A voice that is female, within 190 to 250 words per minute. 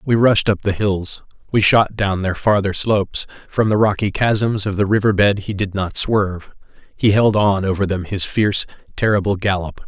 No: male; average, 195 wpm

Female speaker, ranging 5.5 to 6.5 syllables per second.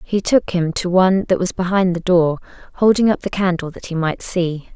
No: female; 5.2 syllables/s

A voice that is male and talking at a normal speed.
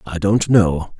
Yes: male; average, 180 wpm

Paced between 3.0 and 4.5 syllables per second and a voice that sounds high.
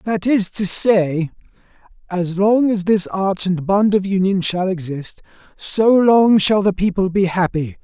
Yes: 4.0 syllables/s; high, 195 Hz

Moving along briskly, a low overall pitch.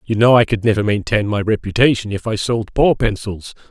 Yes: fast, 210 wpm; low, 110 Hz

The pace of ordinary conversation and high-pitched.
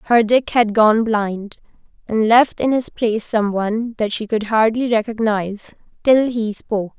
Yes: average, 170 wpm; high, 220 Hz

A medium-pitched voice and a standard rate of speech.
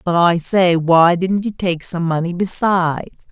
Yes: medium, 175 Hz; average, 180 wpm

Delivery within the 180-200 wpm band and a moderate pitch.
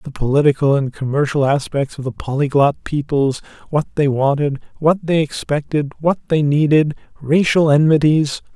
No: average, 140 wpm; medium, 145 Hz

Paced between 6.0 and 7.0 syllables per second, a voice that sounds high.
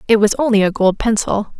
No: 5.6 syllables/s; high, 210 Hz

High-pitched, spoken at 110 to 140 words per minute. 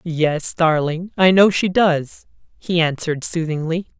No: medium, 165 Hz; slow, 135 wpm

